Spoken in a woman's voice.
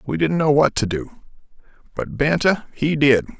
No: male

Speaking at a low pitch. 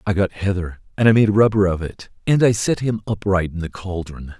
Yes: low, 100 Hz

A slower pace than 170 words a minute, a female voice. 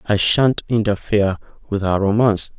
No: average, 140 wpm; male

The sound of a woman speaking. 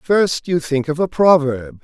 No: male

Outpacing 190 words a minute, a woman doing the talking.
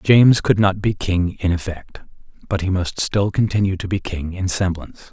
No: average, 200 wpm; male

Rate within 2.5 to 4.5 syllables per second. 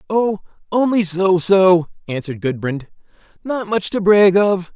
Yes: 4.2 syllables/s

